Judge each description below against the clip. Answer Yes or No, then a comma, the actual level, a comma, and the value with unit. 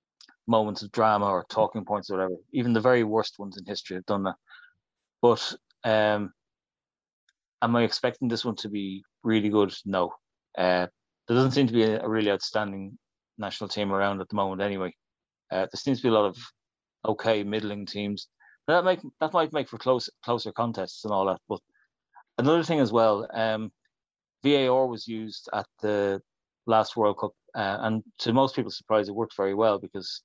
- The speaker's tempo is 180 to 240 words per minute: Yes, average, 190 wpm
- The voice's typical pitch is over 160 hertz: No, low, 110 Hz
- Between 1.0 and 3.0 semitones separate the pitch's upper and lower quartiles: Yes, narrow, 2.6 semitones